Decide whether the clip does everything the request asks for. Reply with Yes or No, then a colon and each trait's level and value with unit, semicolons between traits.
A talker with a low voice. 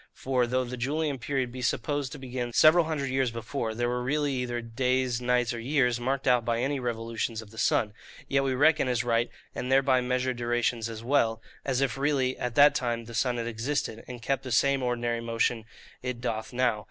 Yes: low, 125 Hz